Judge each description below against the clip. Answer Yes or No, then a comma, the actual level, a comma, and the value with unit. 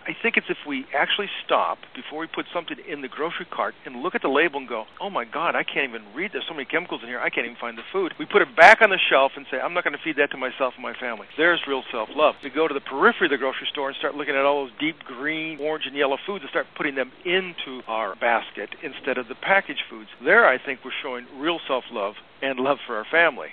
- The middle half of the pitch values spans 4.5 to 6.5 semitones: Yes, average, 4.9 semitones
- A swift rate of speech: Yes, fast, 285 wpm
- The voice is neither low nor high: Yes, medium, 145 Hz